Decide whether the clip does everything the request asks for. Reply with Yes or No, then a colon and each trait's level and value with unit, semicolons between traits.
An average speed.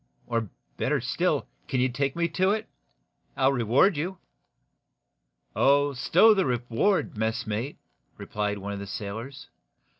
No: slow, 130 wpm